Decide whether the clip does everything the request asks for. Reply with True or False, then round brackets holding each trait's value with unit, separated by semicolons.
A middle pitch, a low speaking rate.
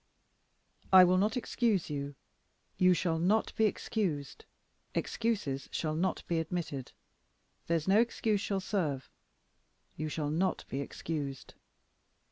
True (175 Hz; 120 wpm)